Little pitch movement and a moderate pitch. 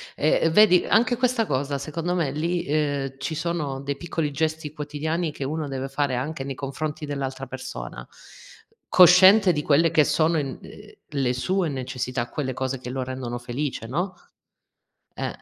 No: average, 3.6 semitones; medium, 145 Hz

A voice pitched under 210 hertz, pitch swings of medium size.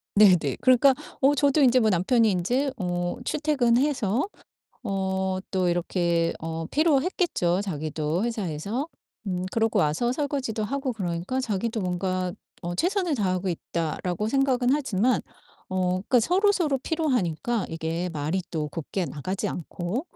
No: high, 200 Hz; wide, 6.9 semitones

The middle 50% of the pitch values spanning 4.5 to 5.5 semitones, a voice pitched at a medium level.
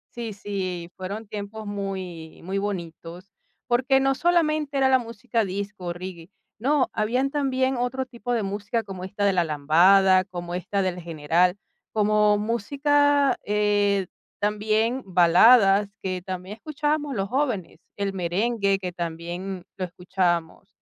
No: average, 4.8 semitones; high, 200 Hz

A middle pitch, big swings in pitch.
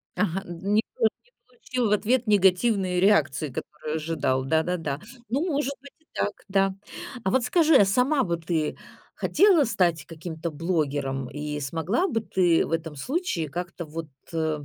Yes: medium, 180 Hz; wide, 6.2 semitones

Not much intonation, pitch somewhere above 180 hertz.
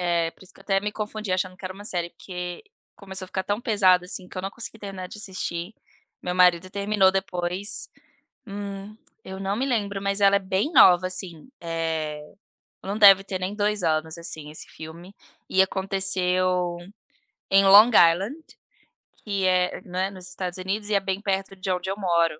Yes: narrow, 1.9 semitones; high, 190 Hz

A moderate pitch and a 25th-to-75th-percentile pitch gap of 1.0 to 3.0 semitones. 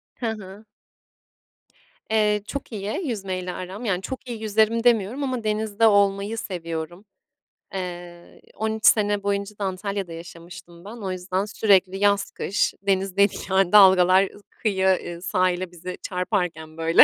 No: high, 195 Hz; narrow, 2.6 semitones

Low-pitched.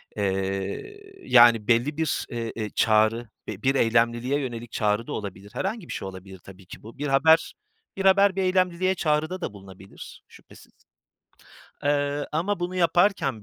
Yes: low, 125 Hz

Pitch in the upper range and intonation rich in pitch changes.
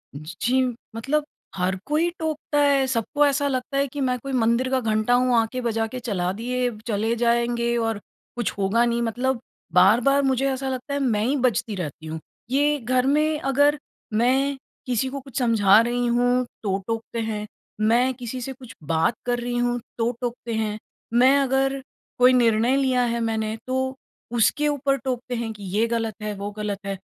No: high, 245 Hz; average, 2.9 semitones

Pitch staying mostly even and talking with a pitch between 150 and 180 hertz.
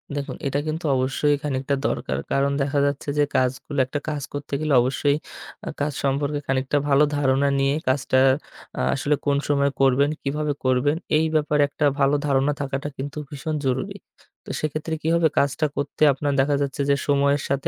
No: narrow, 1.4 semitones; medium, 140 Hz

